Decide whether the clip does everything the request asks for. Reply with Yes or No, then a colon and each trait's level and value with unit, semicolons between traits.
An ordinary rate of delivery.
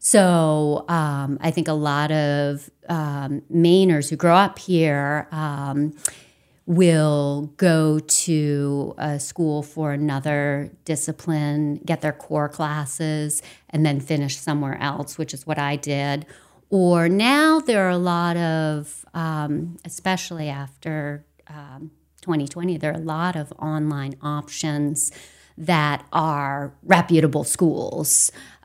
No: slow, 125 wpm